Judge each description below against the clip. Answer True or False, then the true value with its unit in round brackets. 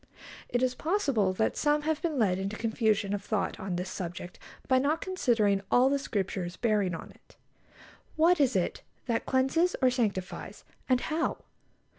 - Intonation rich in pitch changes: True (6.3 semitones)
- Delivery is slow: False (165 wpm)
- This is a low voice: False (235 Hz)